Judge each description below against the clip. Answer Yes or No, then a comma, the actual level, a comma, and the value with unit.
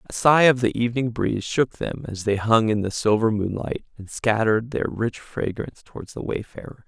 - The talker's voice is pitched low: Yes, low, 115 Hz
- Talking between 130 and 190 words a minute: No, average, 200 wpm